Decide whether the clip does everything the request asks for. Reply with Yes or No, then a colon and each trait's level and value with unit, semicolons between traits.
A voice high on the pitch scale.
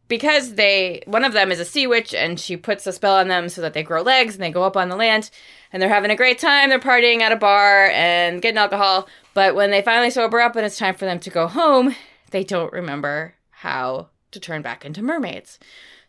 Yes: high, 195 Hz